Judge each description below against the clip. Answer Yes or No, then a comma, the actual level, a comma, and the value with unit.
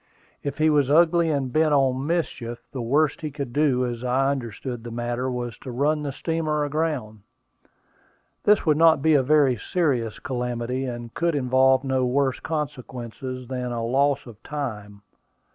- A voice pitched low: Yes, low, 130 Hz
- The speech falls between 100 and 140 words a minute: No, average, 165 wpm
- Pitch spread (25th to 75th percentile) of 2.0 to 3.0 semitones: No, average, 3.5 semitones